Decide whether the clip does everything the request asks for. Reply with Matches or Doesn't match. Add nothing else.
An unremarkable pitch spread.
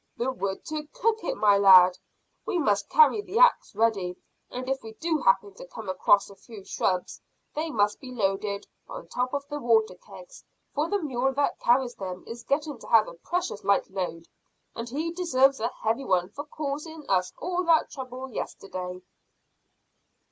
Doesn't match